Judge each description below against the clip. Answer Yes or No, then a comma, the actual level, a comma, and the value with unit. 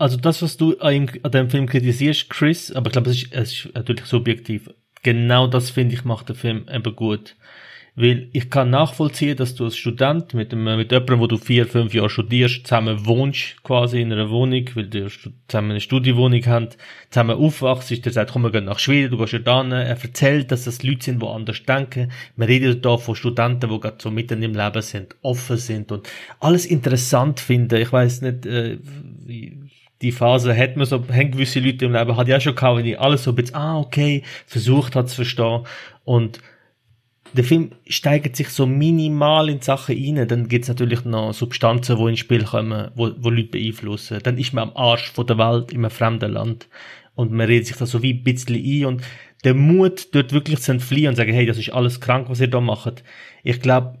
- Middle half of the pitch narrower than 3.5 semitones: Yes, narrow, 2.4 semitones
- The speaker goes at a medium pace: No, fast, 215 wpm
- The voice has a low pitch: Yes, low, 125 Hz